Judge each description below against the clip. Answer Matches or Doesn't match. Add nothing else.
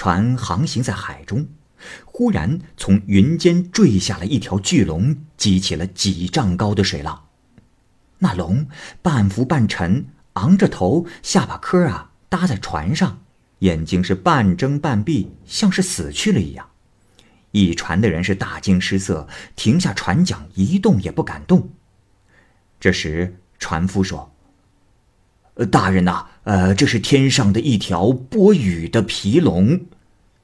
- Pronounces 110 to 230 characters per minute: Matches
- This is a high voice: Doesn't match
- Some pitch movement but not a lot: Doesn't match